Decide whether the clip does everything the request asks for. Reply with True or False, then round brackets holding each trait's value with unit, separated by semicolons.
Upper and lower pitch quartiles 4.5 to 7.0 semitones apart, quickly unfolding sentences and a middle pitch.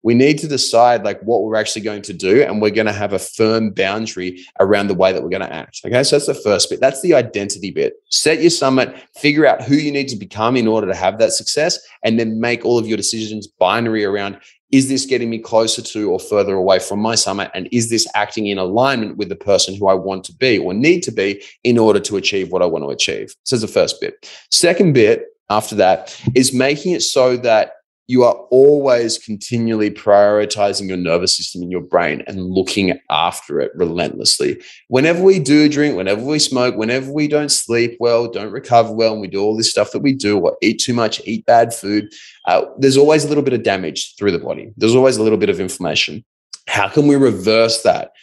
False (5.0 semitones; 230 wpm; 115 Hz)